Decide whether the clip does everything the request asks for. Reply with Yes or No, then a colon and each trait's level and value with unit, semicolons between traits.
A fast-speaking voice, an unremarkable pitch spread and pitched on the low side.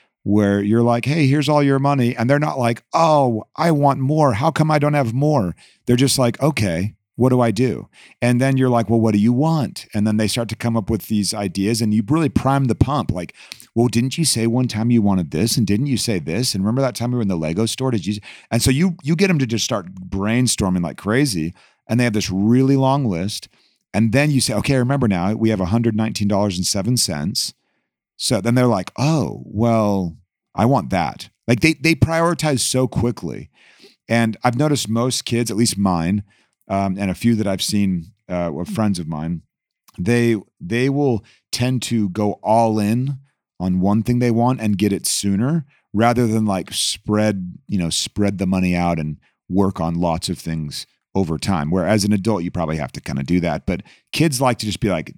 Yes: fast, 215 wpm; average, 4.5 semitones; low, 115 Hz